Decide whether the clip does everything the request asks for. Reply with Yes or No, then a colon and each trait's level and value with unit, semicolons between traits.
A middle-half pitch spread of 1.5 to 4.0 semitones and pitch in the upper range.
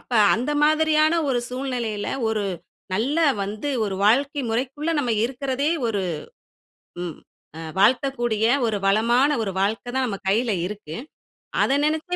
No: average, 4.8 semitones; high, 245 Hz